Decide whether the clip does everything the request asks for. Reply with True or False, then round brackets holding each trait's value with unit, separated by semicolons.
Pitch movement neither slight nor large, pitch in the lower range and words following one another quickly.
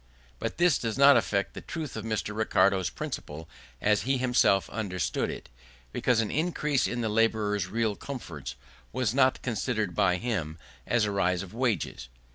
False (4.2 semitones; 110 Hz; 165 wpm)